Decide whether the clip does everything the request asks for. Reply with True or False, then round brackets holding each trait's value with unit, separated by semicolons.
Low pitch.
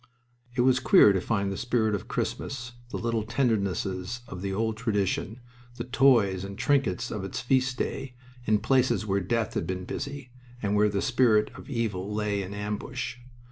True (110 Hz)